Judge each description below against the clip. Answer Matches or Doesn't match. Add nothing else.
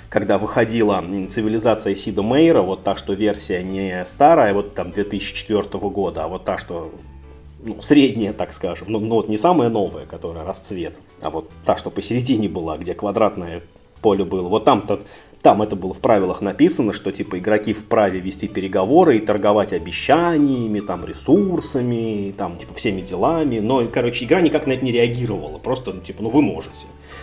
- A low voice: Matches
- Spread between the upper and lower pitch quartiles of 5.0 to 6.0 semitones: Doesn't match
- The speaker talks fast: Matches